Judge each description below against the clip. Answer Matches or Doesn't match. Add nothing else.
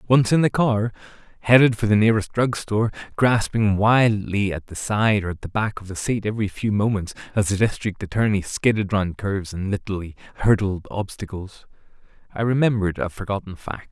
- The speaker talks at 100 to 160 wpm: Doesn't match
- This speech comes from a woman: Doesn't match